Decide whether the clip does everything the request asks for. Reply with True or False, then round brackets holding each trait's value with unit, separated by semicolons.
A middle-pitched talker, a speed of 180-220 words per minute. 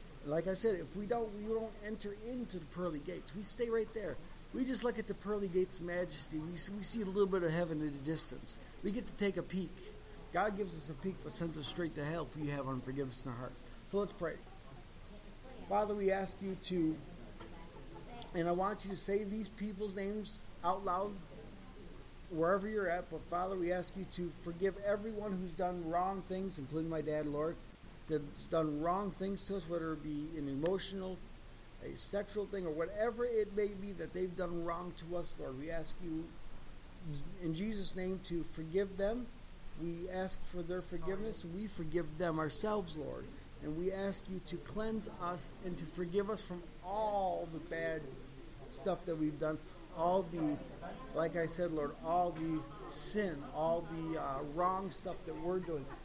True (180 Hz; 195 wpm)